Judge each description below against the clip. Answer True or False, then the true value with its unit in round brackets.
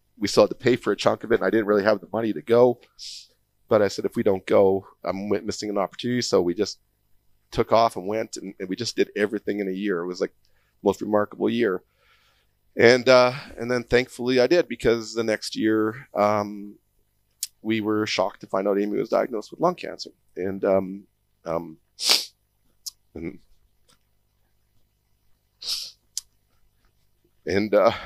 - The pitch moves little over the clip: True (2.2 semitones)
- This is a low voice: True (105 Hz)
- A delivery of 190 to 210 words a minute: False (175 wpm)